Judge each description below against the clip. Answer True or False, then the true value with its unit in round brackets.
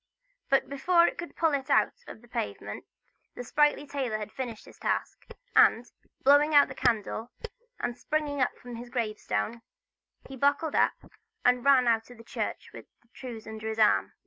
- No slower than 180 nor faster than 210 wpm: True (185 wpm)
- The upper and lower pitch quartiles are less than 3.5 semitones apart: False (4.0 semitones)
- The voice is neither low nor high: False (245 Hz)